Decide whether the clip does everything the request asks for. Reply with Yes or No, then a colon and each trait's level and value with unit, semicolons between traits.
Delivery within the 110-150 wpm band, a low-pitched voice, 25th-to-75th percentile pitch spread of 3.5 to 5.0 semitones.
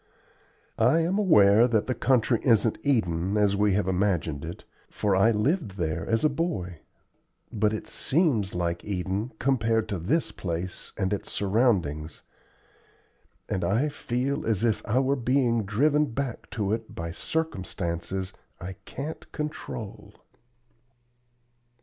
No: slow, 135 wpm; low, 105 Hz; wide, 5.6 semitones